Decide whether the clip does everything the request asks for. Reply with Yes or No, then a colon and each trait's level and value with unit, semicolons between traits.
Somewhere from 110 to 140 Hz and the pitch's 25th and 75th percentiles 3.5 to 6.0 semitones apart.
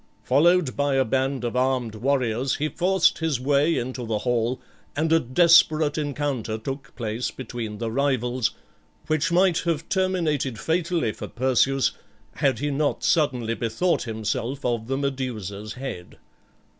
Yes: low, 135 Hz; average, 4.2 semitones